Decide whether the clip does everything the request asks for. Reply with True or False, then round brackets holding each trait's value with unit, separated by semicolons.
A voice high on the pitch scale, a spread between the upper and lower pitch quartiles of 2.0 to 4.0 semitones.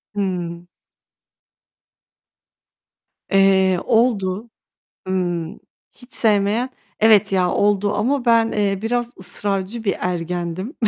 True (200 Hz; 3.4 semitones)